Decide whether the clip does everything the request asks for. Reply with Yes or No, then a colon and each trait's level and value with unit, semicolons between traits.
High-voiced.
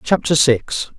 No: medium, 140 Hz